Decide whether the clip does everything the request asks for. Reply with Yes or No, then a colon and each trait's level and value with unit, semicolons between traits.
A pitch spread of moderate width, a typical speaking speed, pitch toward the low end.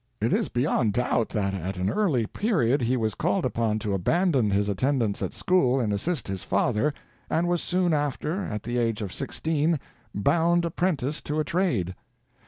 No: wide, 7.6 semitones; average, 180 wpm; low, 130 Hz